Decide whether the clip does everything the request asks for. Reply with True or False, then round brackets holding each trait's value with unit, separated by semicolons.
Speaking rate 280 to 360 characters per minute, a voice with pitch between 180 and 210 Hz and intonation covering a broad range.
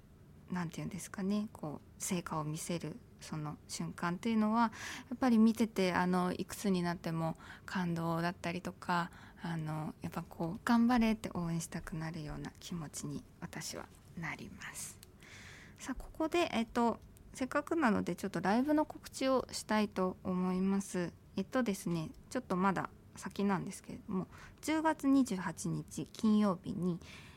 False (315 characters per minute; 190 Hz; 5.0 semitones)